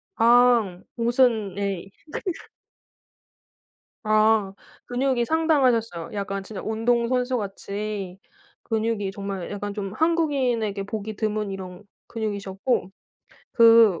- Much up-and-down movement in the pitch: No, average, 3.4 semitones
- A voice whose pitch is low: No, high, 215 Hz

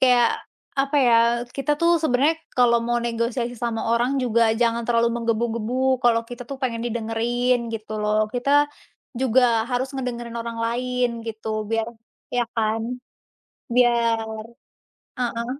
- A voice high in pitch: Yes, high, 235 Hz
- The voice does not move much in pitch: Yes, narrow, 1.3 semitones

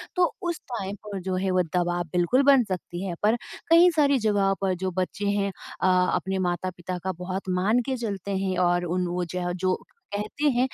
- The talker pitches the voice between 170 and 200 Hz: Yes, high, 190 Hz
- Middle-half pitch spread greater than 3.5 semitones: No, average, 2.7 semitones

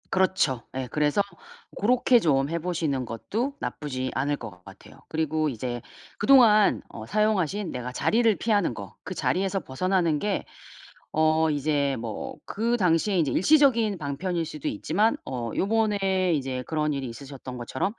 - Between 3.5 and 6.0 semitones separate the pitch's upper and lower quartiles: No, wide, 7.3 semitones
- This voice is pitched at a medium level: Yes, medium, 160 Hz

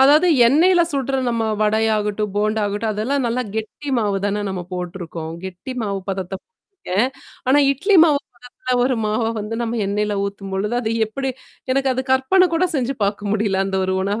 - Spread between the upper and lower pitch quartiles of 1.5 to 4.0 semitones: No, average, 4.7 semitones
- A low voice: No, high, 220 Hz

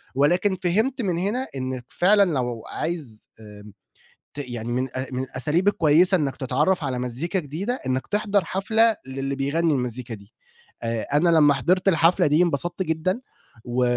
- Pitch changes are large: Yes, wide, 6.2 semitones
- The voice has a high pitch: No, medium, 150 Hz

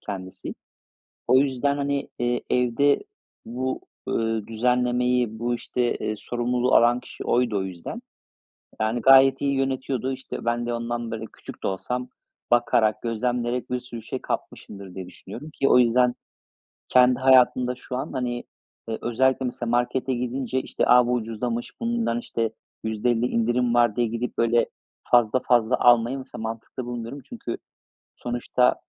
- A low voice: Yes, low, 120 Hz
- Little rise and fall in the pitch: Yes, narrow, 1.6 semitones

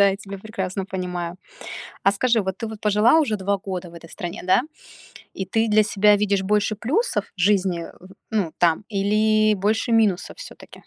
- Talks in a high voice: Yes, high, 200 Hz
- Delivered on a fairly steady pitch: Yes, narrow, 2.3 semitones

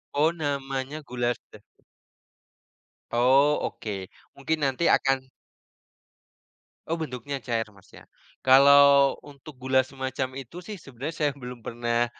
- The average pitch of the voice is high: No, low, 135 Hz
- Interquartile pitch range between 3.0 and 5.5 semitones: No, narrow, 2.4 semitones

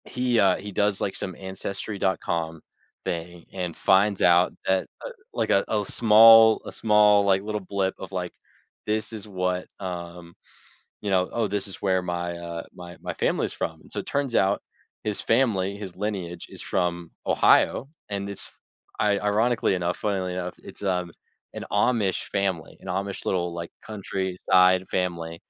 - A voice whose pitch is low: Yes, very low, 95 Hz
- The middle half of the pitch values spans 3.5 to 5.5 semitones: No, narrow, 2.5 semitones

